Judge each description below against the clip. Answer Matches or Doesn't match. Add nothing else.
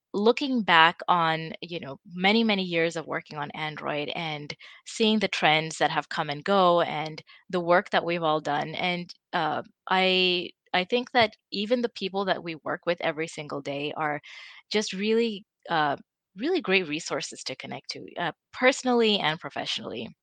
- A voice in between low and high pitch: Matches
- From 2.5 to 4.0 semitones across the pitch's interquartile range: Doesn't match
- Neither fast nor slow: Matches